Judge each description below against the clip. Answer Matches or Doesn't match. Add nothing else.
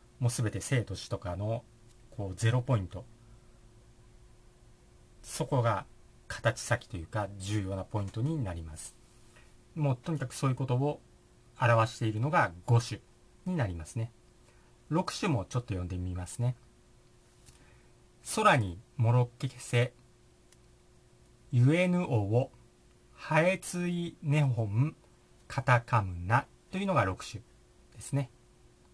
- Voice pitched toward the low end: Matches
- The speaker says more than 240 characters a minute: Doesn't match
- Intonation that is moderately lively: Matches